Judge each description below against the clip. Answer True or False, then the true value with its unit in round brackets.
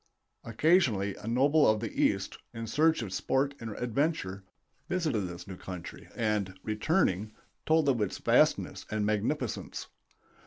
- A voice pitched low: True (110 Hz)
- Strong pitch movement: True (5.9 semitones)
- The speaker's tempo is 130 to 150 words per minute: True (140 wpm)